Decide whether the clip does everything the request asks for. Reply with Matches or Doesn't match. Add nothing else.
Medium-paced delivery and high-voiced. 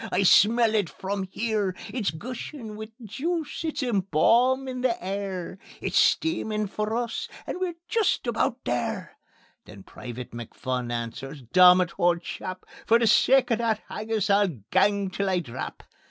Matches